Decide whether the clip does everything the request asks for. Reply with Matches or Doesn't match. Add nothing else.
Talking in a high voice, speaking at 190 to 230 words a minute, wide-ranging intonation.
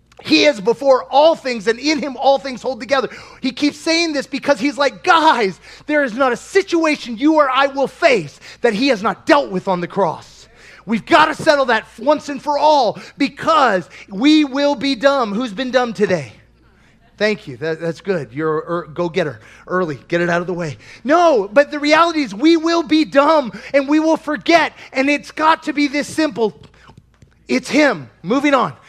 Matches